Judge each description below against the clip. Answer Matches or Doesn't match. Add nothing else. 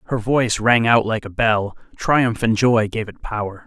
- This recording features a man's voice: Matches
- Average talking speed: Doesn't match